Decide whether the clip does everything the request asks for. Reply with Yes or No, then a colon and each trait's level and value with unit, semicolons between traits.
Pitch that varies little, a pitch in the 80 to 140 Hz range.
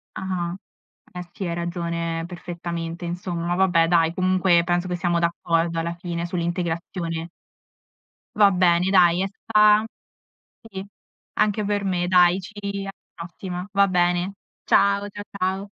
No: narrow, 1.9 semitones; medium, 175 Hz